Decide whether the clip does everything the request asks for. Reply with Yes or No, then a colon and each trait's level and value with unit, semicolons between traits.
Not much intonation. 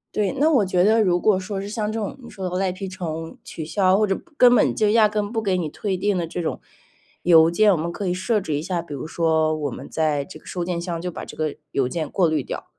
No: average, 4.1 semitones